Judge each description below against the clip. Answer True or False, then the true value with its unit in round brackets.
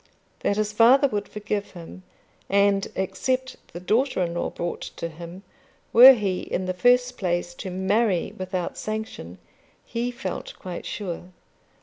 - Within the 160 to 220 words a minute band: False (145 wpm)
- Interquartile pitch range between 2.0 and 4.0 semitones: False (4.4 semitones)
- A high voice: True (200 Hz)